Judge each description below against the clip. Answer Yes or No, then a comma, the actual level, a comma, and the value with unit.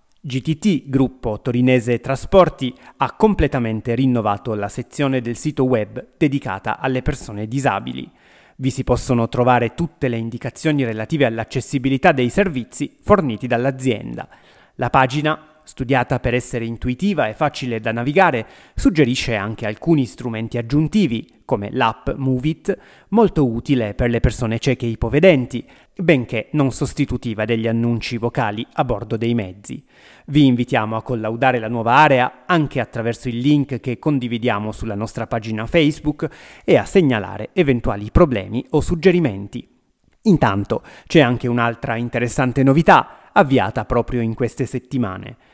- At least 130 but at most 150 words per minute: Yes, average, 135 wpm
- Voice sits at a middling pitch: No, low, 125 Hz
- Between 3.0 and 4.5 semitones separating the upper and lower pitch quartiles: Yes, average, 3.5 semitones